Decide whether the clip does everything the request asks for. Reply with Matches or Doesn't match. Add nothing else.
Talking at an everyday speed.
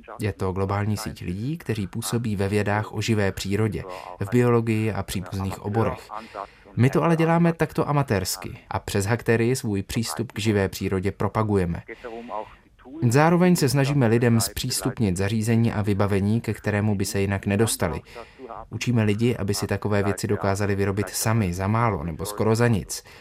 Matches